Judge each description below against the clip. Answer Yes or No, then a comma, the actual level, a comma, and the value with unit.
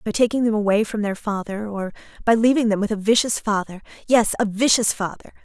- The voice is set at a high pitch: Yes, high, 215 Hz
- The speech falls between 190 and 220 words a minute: Yes, average, 200 wpm